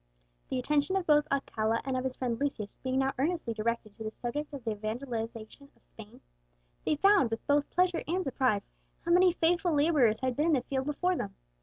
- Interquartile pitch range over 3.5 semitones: Yes, average, 5.0 semitones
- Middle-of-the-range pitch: No, very high, 270 Hz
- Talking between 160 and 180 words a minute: No, fast, 205 wpm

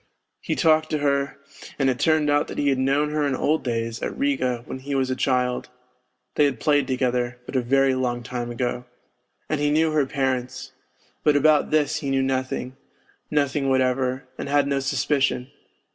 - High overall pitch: No, low, 135 Hz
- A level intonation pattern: Yes, narrow, 2.3 semitones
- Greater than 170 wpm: Yes, average, 190 wpm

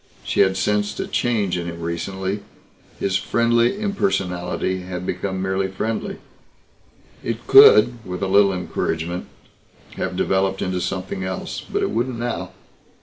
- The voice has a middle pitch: No, very low, 95 Hz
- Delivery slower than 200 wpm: Yes, average, 140 wpm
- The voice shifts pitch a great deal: No, average, 3.9 semitones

